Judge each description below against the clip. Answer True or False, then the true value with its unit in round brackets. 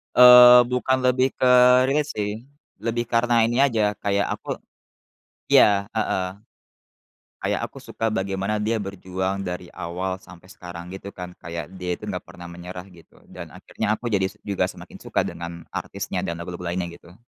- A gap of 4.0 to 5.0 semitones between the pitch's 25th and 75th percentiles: True (4.5 semitones)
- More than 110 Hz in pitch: False (100 Hz)